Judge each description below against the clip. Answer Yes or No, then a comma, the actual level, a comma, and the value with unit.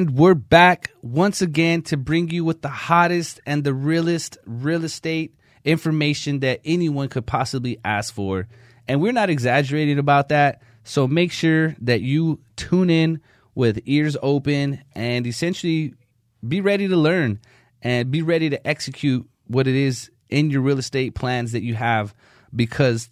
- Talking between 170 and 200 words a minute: No, average, 160 wpm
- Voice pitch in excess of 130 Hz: Yes, medium, 140 Hz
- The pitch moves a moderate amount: Yes, average, 4.8 semitones